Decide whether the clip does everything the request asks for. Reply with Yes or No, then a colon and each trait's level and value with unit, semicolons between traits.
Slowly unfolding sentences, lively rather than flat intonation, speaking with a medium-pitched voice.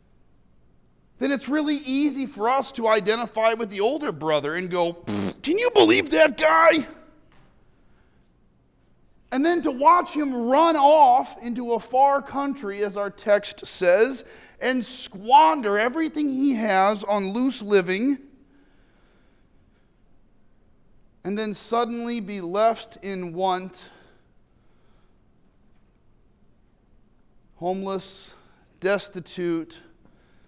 No: slow, 100 wpm; wide, 6.9 semitones; high, 220 Hz